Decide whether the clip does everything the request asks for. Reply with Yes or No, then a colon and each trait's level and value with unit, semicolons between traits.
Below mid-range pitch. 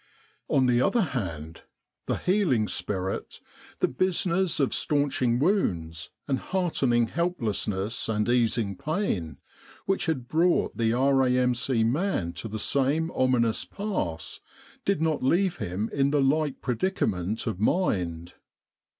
Yes: low, 125 Hz